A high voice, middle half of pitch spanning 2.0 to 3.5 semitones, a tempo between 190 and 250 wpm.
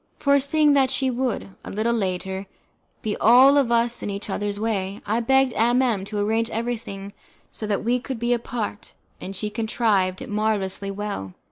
No: high, 220 Hz; average, 3.2 semitones; average, 175 wpm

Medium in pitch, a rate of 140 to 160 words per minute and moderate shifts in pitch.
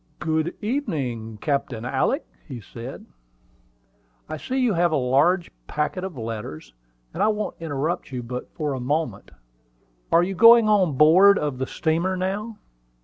No: medium, 150 Hz; average, 150 wpm; wide, 7.7 semitones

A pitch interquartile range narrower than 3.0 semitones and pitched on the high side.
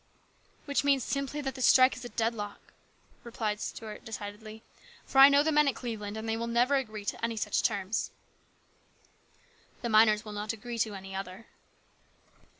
No: average, 3.4 semitones; high, 225 Hz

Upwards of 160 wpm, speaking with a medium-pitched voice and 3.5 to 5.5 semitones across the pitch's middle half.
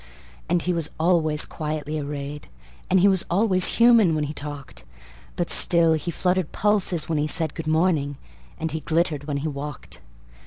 No: average, 170 wpm; medium, 160 Hz; average, 3.1 semitones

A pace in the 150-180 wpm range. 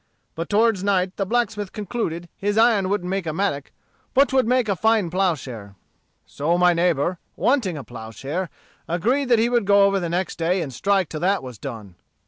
No: average, 190 wpm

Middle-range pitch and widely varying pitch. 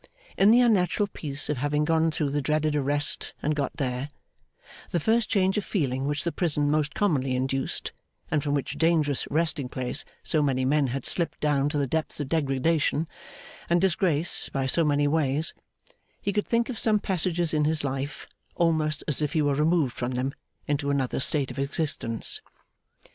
No: medium, 150 Hz; average, 3.2 semitones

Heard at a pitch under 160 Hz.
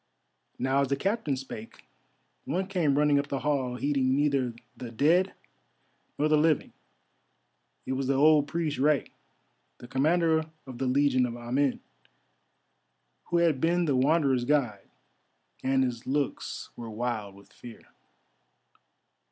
Yes: medium, 140 Hz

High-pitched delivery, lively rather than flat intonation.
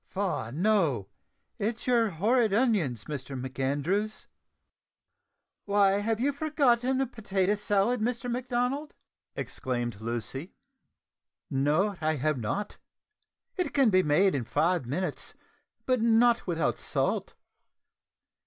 Yes: high, 200 Hz; wide, 8.3 semitones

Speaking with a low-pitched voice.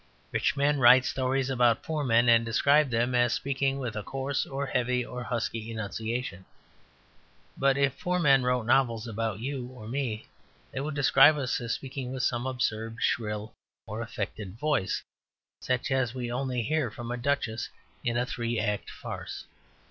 Yes: low, 125 Hz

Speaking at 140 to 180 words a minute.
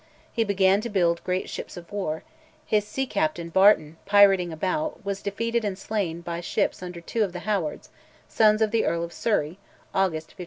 No: average, 190 wpm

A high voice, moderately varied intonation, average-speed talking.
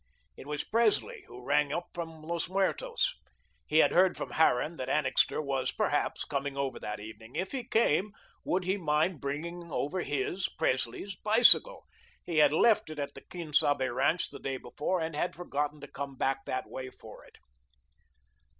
No: medium, 155 Hz; average, 4.6 semitones; average, 175 wpm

